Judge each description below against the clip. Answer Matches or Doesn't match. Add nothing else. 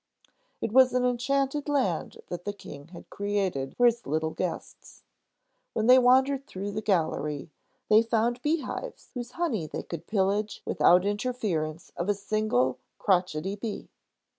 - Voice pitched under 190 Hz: Doesn't match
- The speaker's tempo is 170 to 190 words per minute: Doesn't match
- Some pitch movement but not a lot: Doesn't match